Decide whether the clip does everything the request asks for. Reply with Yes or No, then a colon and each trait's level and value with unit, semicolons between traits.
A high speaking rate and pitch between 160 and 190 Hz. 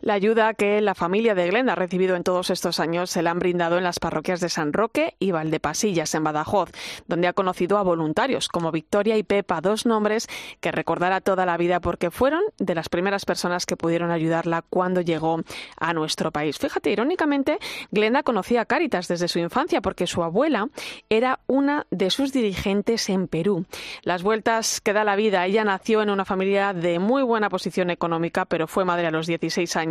Yes: fast, 200 wpm; medium, 185 Hz